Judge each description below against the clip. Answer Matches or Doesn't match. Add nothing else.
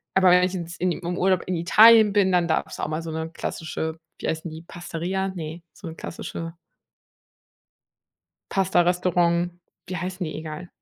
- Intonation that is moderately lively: Doesn't match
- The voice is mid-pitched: Matches